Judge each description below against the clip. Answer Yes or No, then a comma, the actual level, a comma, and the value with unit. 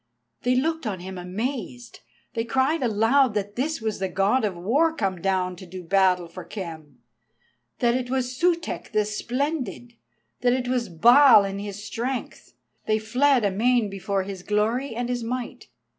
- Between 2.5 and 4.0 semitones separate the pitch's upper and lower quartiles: No, average, 4.6 semitones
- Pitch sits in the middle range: No, high, 225 Hz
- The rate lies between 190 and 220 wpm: No, average, 165 wpm